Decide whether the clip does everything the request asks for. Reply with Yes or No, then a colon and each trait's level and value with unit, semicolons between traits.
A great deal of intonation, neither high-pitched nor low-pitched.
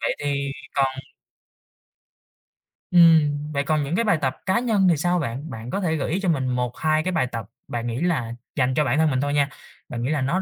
No: average, 4.5 semitones; medium, 145 Hz